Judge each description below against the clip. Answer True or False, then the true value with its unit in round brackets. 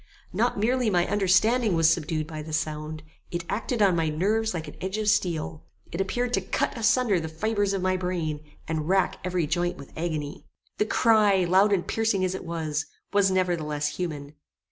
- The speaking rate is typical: True (190 wpm)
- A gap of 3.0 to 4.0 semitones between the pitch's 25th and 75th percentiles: False (4.4 semitones)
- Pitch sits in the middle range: True (180 Hz)